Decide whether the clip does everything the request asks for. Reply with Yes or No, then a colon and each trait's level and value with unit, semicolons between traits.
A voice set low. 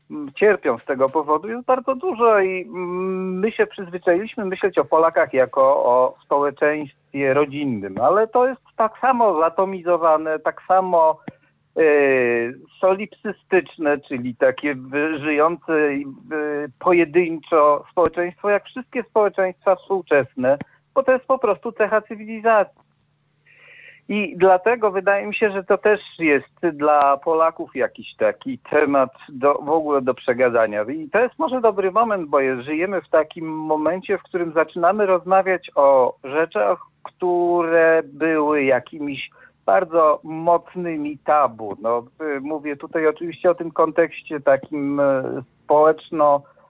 No: medium, 165 Hz